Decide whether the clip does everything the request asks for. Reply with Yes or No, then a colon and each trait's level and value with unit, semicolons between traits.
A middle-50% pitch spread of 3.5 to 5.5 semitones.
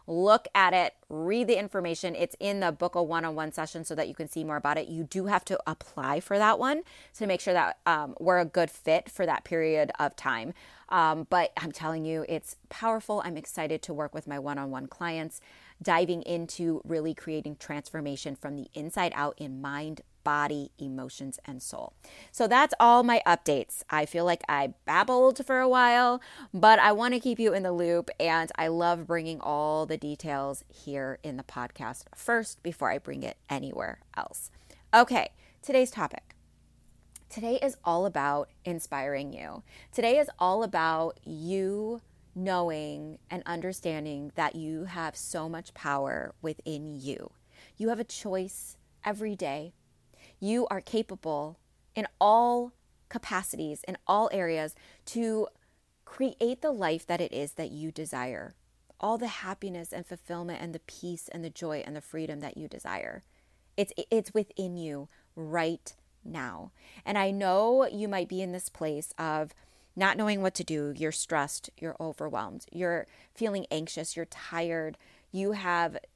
Yes: average, 4.4 semitones